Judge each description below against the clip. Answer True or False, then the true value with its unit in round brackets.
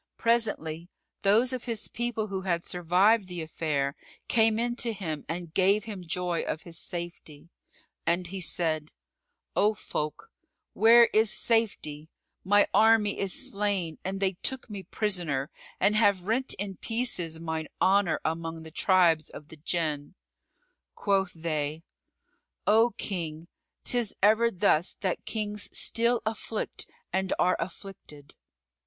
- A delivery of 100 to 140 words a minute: True (135 wpm)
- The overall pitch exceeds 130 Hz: True (190 Hz)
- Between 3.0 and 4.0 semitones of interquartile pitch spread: False (4.7 semitones)